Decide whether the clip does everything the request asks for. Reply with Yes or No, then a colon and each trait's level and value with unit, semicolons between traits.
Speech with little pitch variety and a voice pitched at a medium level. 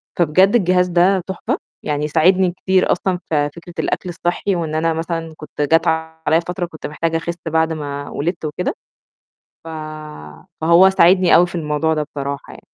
Yes: narrow, 2.3 semitones; medium, 165 Hz